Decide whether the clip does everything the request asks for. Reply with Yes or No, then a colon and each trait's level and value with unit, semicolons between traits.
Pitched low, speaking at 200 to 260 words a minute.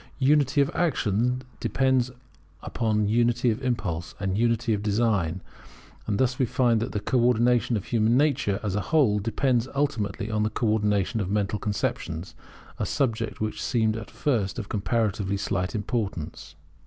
No: low, 110 Hz; average, 160 wpm